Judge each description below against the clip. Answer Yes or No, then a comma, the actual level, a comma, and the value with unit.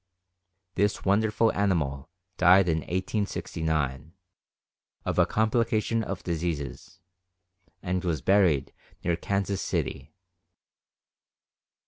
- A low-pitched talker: Yes, very low, 90 Hz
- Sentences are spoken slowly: Yes, slow, 85 wpm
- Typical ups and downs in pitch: Yes, average, 4.0 semitones